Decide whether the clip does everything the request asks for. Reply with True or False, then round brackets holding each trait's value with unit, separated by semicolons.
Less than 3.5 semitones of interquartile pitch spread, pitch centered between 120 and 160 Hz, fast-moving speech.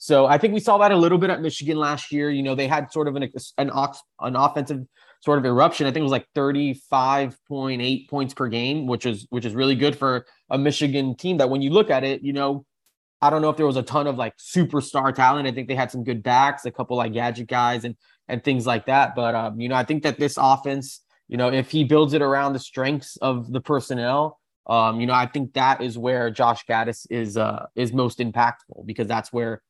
True (2.7 semitones; 135 Hz; 245 wpm)